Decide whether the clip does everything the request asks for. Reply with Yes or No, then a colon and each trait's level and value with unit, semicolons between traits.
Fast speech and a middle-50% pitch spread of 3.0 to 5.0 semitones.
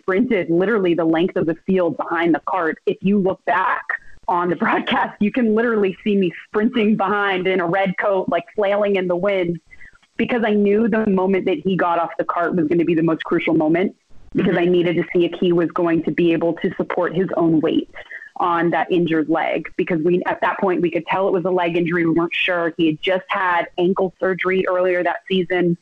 No: fast, 230 wpm; narrow, 2.4 semitones